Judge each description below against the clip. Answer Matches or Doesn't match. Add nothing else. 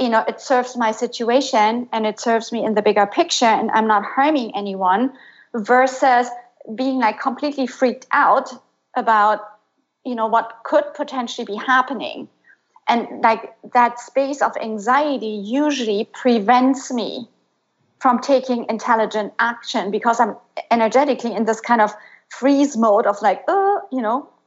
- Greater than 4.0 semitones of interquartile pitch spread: Doesn't match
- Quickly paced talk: Doesn't match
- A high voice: Matches